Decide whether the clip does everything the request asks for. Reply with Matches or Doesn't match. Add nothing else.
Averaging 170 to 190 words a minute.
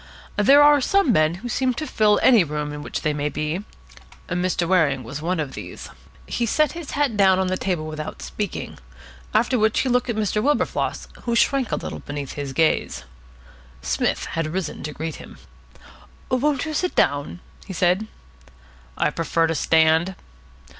Matches